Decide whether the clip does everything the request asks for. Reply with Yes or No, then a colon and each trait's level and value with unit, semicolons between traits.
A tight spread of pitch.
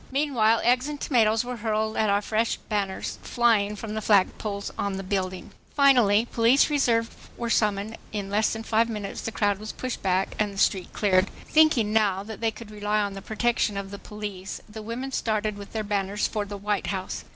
Yes: narrow, 2.2 semitones